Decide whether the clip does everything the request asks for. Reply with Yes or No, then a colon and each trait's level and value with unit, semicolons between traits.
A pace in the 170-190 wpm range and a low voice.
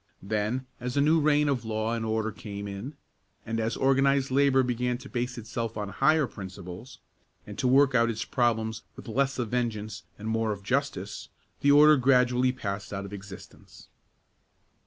Yes: average, 175 wpm; low, 120 Hz